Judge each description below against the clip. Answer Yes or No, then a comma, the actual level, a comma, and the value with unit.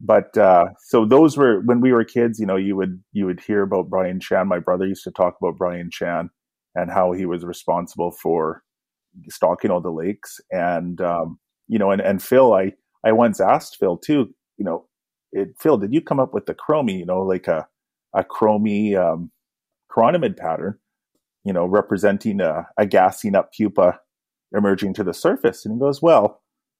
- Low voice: Yes, very low, 95 Hz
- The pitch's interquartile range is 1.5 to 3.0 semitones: No, average, 3.6 semitones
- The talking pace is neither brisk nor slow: Yes, average, 195 wpm